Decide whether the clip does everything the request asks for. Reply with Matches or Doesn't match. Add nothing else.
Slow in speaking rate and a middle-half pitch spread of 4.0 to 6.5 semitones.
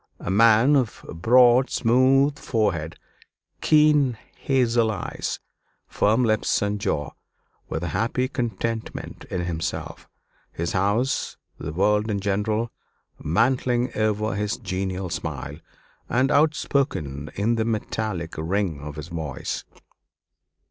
Matches